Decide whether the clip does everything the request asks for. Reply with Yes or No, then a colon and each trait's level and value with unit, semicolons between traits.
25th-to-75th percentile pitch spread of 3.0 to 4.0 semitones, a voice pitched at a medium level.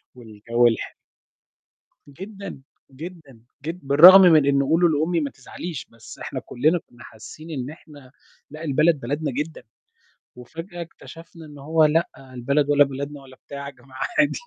Yes: average, 3.6 semitones; medium, 145 Hz